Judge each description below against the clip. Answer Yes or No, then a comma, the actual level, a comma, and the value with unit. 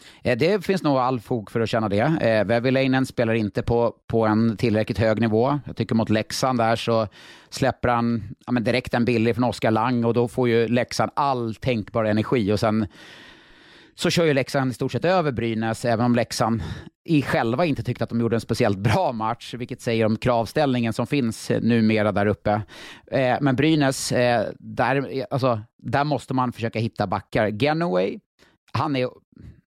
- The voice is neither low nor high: No, low, 120 Hz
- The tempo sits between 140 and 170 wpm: No, average, 185 wpm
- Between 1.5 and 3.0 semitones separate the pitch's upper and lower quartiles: Yes, narrow, 2.6 semitones